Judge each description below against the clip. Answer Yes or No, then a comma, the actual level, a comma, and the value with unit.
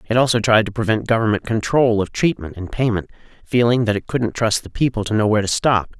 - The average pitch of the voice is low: Yes, low, 110 Hz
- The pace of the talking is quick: Yes, fast, 230 wpm